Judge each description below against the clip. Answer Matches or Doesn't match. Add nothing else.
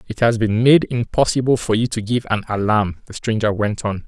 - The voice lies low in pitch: Matches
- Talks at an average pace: Doesn't match